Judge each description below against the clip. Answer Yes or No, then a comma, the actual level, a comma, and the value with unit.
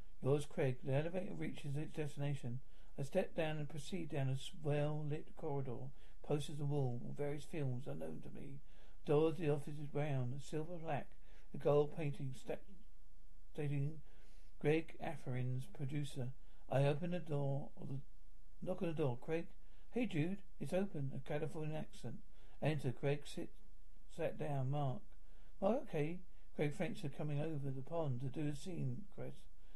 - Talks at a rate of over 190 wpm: No, average, 165 wpm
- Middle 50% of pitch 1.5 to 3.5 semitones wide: Yes, average, 2.7 semitones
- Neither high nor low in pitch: Yes, medium, 145 Hz